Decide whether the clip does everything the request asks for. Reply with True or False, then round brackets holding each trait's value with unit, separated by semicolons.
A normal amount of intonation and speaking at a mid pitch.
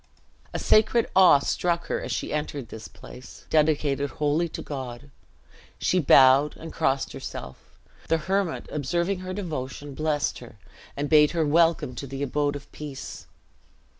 True (3.4 semitones; 150 Hz)